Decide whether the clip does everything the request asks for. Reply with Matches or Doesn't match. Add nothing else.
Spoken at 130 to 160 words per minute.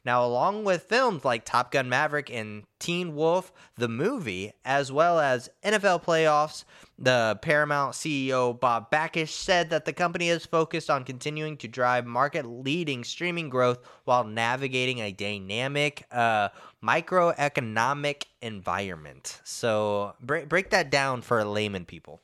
Matches